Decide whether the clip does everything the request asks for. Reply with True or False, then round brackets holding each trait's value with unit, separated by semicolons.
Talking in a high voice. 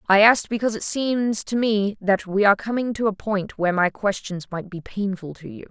True (205 Hz)